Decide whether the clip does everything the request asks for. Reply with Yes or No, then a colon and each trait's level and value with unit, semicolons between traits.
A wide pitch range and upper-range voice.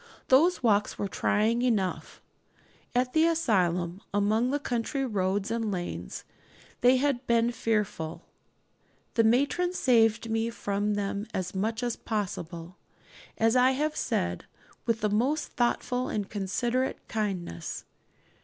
No: average, 3.7 semitones; high, 225 Hz